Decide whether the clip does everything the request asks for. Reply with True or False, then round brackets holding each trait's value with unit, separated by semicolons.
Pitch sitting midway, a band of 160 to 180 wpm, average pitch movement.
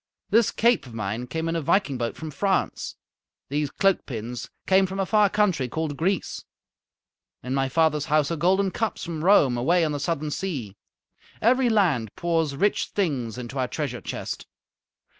False (160 Hz; 175 wpm; 6.3 semitones)